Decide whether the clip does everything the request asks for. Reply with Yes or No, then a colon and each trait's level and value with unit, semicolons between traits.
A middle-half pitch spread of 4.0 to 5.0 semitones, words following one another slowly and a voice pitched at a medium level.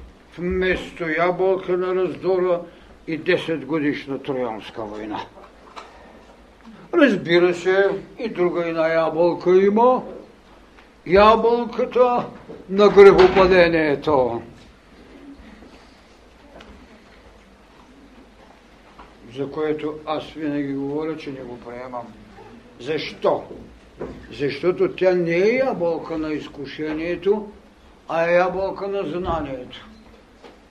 Yes: average, 4.4 semitones; slow, 80 wpm; medium, 170 Hz